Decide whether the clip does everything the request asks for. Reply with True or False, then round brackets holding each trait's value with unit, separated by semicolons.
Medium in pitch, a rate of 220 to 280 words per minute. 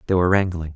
False (90 Hz; 240 wpm)